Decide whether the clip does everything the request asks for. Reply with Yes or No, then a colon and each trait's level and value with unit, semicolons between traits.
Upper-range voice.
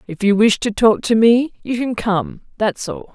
Yes: high, 220 Hz